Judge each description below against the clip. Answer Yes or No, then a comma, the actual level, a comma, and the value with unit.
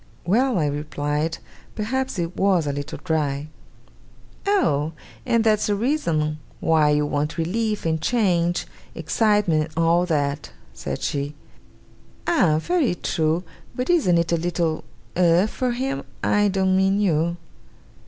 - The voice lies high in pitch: No, medium, 170 Hz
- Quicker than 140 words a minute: No, slow, 135 wpm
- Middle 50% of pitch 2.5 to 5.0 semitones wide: No, wide, 5.4 semitones